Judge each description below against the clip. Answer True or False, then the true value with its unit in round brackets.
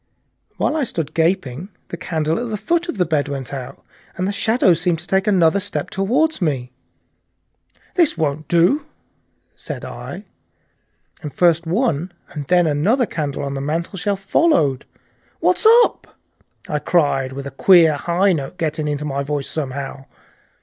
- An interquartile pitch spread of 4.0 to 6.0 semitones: True (5.3 semitones)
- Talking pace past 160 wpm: False (155 wpm)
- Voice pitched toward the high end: False (165 Hz)